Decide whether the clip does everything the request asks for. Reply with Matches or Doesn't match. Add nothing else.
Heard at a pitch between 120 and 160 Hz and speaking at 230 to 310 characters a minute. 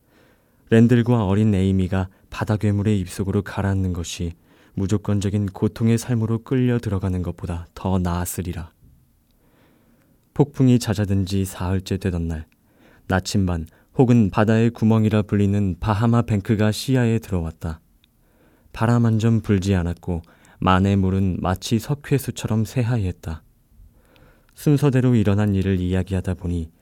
Doesn't match